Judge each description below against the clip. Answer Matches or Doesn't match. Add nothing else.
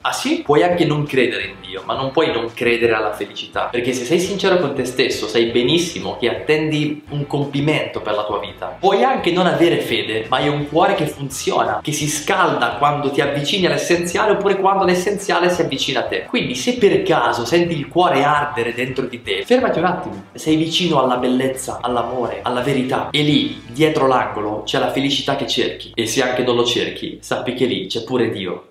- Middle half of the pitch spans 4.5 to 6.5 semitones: Matches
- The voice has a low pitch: Doesn't match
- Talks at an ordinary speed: Doesn't match